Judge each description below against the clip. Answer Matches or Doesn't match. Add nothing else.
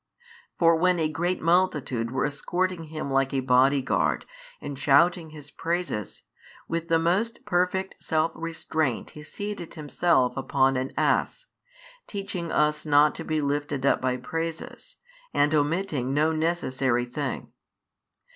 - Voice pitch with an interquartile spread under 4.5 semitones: Matches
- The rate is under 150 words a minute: Matches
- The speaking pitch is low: Doesn't match